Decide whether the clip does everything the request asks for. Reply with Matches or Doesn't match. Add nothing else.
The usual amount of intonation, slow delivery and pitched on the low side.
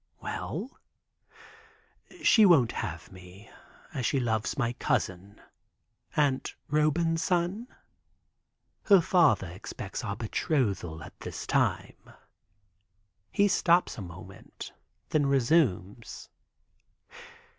Doesn't match